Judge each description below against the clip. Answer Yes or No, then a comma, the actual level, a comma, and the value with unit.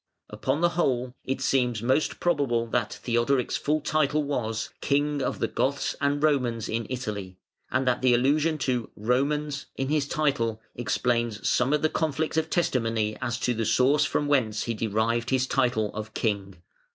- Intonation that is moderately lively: Yes, average, 4.0 semitones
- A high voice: No, low, 125 Hz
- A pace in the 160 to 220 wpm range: Yes, average, 170 wpm